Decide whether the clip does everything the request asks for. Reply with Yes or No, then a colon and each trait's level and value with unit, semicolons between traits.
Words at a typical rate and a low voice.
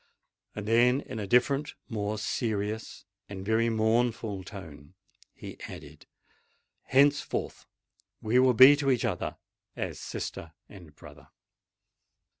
No: slow, 100 wpm; low, 110 Hz